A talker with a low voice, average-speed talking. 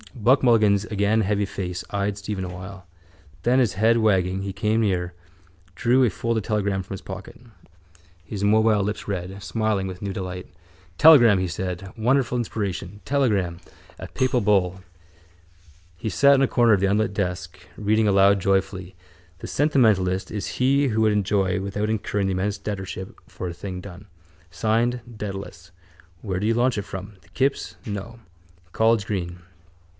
Yes: low, 100 Hz; average, 160 wpm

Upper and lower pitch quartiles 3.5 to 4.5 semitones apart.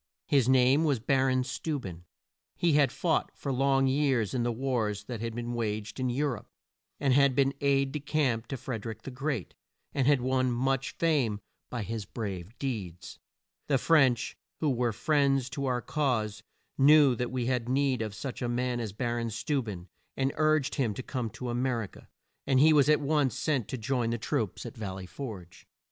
No: average, 3.1 semitones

